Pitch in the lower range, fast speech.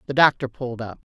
Yes: low, 125 Hz; fast, 215 wpm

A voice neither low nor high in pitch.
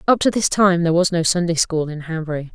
Yes: medium, 170 Hz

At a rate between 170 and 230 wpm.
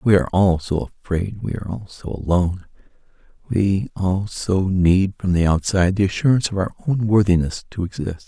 Yes: average, 180 wpm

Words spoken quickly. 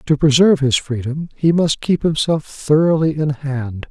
No: average, 170 wpm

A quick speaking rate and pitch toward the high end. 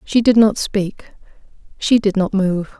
No: average, 170 wpm; high, 205 Hz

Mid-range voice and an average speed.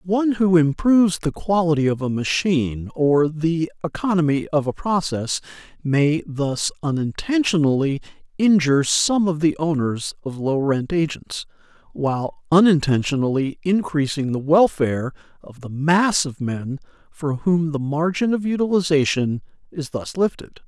No: medium, 155 Hz; slow, 130 wpm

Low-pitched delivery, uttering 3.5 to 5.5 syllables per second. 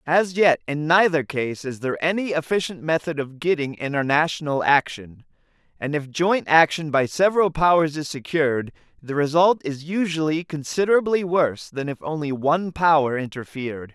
No: medium, 155 Hz; 5.2 syllables/s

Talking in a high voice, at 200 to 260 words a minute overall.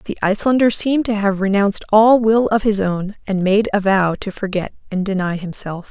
Yes: high, 205 Hz; fast, 205 wpm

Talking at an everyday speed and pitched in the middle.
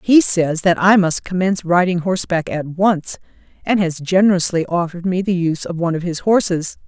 Yes: average, 190 wpm; medium, 180 Hz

